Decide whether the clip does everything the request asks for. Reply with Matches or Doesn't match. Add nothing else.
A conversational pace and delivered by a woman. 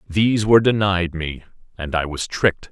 Doesn't match